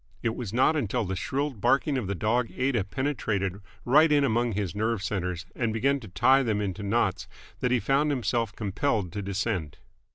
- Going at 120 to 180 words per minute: No, average, 190 wpm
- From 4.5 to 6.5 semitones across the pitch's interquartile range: Yes, average, 4.8 semitones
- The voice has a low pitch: Yes, low, 115 Hz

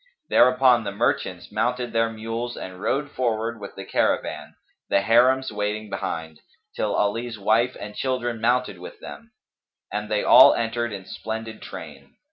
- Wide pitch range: No, average, 2.7 semitones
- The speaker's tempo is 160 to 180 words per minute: No, average, 150 wpm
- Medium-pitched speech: No, low, 115 Hz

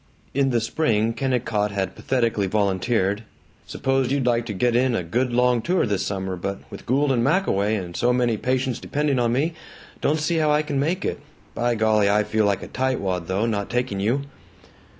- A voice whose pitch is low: Yes, low, 120 Hz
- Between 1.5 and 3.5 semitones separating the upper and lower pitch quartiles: No, average, 4.3 semitones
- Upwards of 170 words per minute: Yes, average, 200 wpm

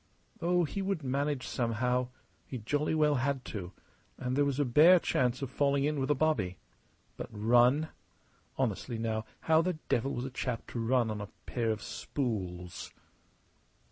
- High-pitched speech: No, low, 130 Hz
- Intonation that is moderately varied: Yes, average, 4.3 semitones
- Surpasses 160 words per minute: Yes, average, 170 wpm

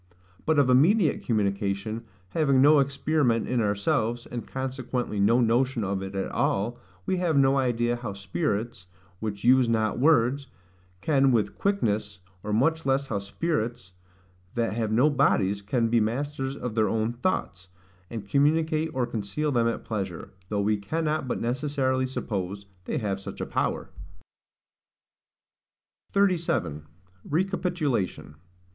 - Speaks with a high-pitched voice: No, low, 120 Hz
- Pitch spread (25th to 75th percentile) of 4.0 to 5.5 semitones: Yes, average, 5.0 semitones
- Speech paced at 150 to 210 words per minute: No, average, 140 wpm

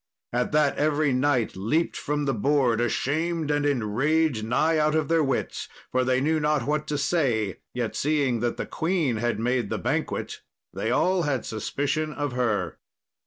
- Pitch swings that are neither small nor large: Yes, average, 4.1 semitones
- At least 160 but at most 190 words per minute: Yes, average, 170 wpm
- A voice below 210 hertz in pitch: Yes, medium, 140 Hz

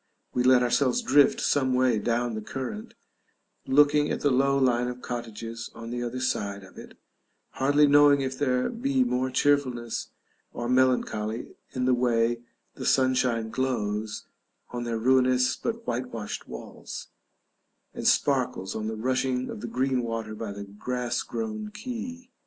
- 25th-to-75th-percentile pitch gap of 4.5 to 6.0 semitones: No, average, 2.8 semitones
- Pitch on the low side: Yes, low, 125 Hz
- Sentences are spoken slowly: No, average, 150 wpm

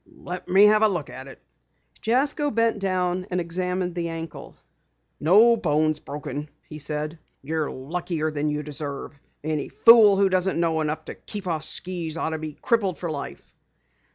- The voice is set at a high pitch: No, medium, 170 Hz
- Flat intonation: No, average, 3.8 semitones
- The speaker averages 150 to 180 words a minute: Yes, average, 170 wpm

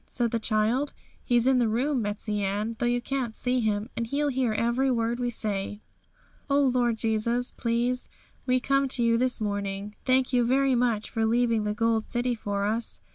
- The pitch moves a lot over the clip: No, narrow, 2.5 semitones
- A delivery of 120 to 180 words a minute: No, average, 190 wpm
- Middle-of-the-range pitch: No, high, 235 Hz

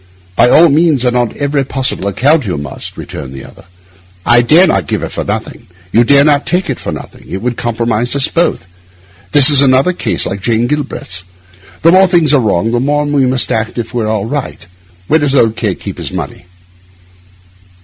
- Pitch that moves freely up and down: No, average, 4.7 semitones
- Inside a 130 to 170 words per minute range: No, fast, 205 wpm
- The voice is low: Yes, low, 125 Hz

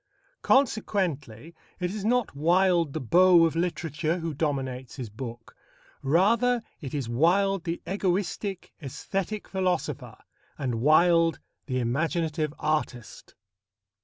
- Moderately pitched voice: Yes, medium, 165 Hz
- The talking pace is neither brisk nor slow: No, slow, 110 wpm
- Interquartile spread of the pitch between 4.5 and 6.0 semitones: Yes, average, 5.2 semitones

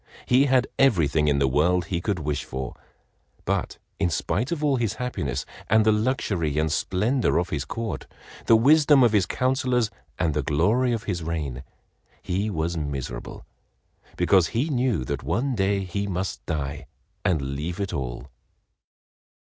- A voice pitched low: Yes, very low, 90 Hz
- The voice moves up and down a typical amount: No, wide, 7.6 semitones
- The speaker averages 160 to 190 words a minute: Yes, average, 165 wpm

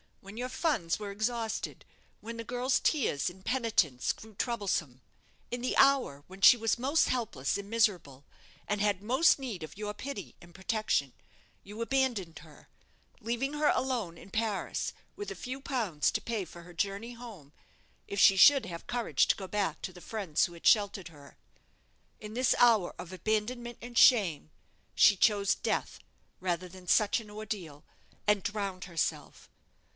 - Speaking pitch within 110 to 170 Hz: No, high, 210 Hz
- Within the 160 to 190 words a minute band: Yes, average, 165 wpm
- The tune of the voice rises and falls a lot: No, average, 4.8 semitones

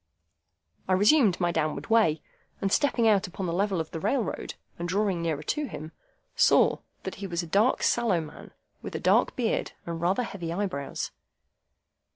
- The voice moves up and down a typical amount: Yes, average, 4.0 semitones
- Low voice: No, medium, 185 Hz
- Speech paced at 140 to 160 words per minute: No, average, 175 wpm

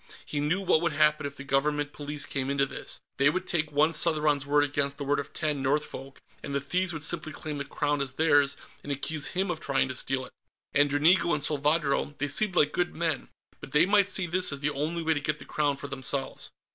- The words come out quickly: Yes, fast, 235 wpm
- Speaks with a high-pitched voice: No, medium, 145 Hz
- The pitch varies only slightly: Yes, narrow, 2.1 semitones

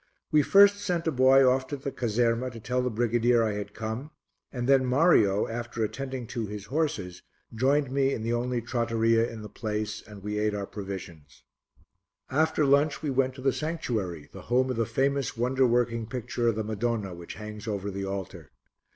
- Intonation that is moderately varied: Yes, average, 3.7 semitones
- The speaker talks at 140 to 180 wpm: No, average, 195 wpm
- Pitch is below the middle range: Yes, low, 120 Hz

